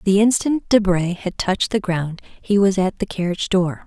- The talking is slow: No, average, 200 wpm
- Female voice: Yes, female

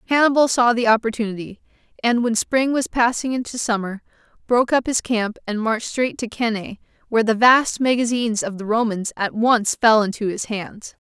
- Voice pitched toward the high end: Yes, high, 230 Hz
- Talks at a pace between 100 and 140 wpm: No, average, 180 wpm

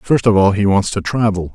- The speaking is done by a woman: No, male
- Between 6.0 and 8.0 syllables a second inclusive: No, 5.3 syllables/s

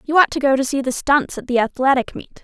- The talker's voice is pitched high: Yes, very high, 265 Hz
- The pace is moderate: No, fast, 295 wpm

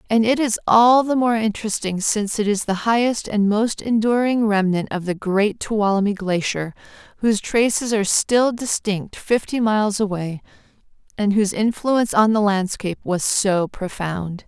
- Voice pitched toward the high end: Yes, high, 210 Hz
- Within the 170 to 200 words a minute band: No, average, 160 wpm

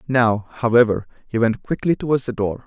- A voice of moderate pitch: No, low, 120 Hz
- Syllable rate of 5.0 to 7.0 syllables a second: Yes, 5.5 syllables/s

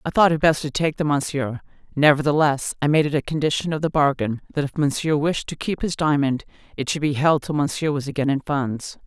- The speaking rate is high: Yes, fast, 230 wpm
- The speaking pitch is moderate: Yes, medium, 145 Hz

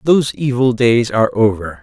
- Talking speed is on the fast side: No, average, 165 wpm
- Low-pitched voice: Yes, low, 120 Hz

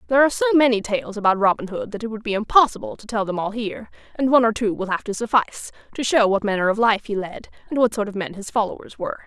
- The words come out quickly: Yes, fast, 270 wpm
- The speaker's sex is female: Yes, female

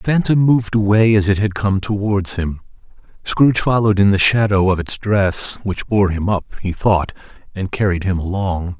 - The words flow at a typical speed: Yes, average, 190 wpm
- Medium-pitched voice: No, low, 100 Hz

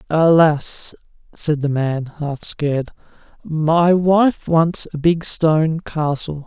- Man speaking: Yes, male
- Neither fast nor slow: No, slow, 120 wpm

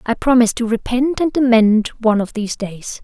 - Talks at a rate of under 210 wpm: Yes, average, 200 wpm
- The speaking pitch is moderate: No, high, 235 Hz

